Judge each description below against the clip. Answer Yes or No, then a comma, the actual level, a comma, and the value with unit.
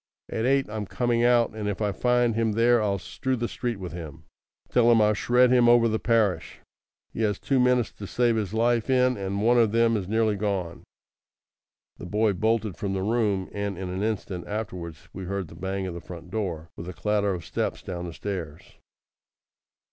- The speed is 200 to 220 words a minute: Yes, fast, 205 wpm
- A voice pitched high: No, low, 105 Hz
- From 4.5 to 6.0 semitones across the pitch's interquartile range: No, average, 3.7 semitones